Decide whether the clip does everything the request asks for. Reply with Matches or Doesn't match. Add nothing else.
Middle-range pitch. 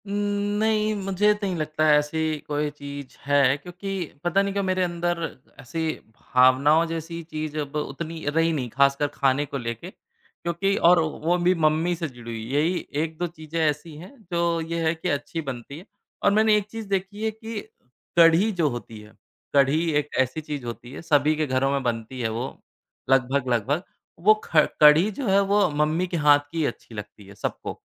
Matches